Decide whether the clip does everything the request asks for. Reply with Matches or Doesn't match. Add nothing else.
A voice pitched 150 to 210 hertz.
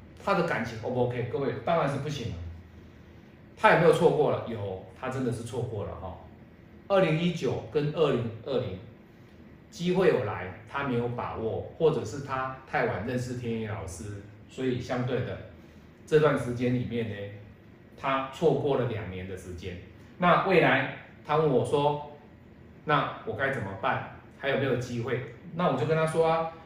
Doesn't match